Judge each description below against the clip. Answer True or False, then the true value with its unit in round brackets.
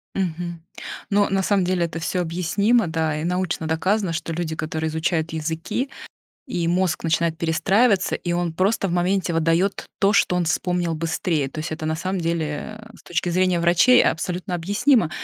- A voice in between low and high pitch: True (175 Hz)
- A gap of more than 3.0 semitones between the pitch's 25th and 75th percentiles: False (2.7 semitones)